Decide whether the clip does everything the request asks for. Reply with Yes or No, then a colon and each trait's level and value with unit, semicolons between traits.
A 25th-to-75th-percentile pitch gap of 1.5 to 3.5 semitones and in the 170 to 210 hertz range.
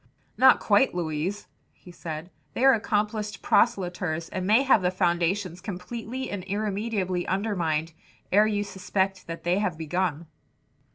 Yes: average, 3.2 semitones; high, 190 Hz